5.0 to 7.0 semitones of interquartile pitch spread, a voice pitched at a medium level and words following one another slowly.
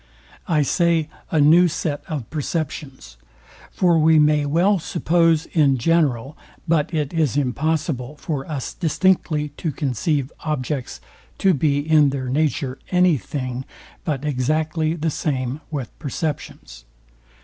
No: average, 2.9 semitones; medium, 150 Hz; slow, 125 wpm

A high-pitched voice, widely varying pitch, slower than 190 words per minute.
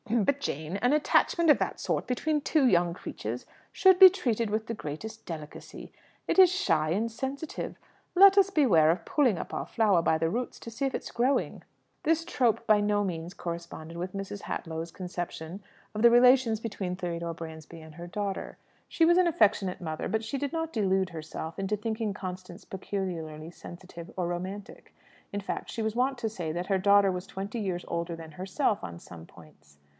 No: high, 200 Hz; wide, 5.9 semitones; average, 200 wpm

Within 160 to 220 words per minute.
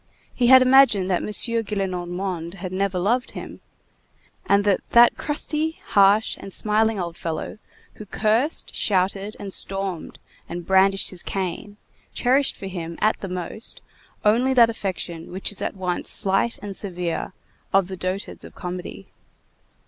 No: average, 150 wpm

